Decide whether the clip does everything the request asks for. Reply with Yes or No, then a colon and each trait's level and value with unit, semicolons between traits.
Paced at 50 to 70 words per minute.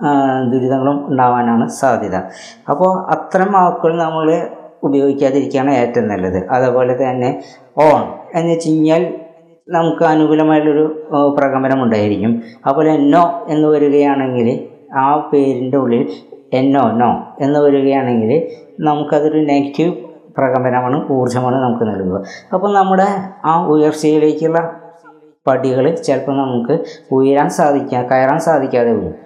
No: average, 100 wpm